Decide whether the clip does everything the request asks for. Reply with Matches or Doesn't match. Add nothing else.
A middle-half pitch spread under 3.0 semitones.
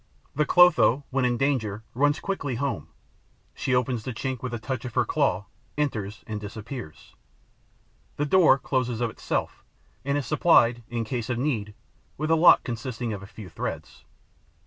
Doesn't match